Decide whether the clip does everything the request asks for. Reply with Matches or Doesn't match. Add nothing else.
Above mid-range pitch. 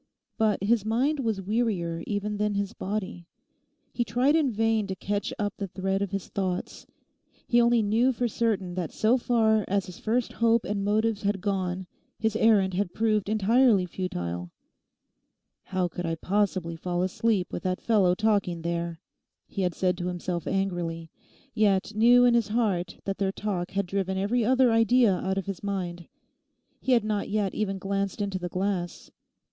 Matches